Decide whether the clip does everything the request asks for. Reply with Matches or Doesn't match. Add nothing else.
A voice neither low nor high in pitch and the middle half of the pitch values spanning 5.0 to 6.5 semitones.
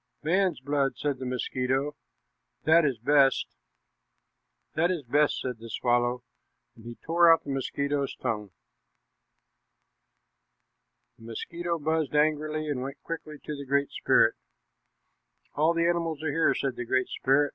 Doesn't match